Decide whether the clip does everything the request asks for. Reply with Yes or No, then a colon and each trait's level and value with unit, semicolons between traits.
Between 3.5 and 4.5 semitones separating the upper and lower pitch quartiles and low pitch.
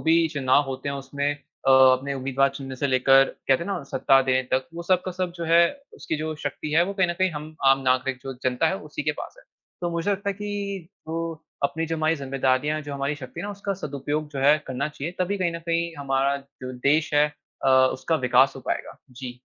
No: average, 3.8 semitones; medium, 145 Hz